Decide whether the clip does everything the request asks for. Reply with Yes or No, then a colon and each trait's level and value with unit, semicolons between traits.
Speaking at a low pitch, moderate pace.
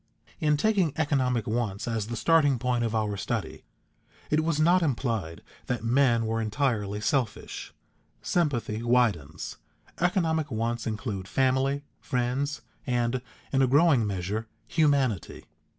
No: low, 125 Hz; slow, 125 wpm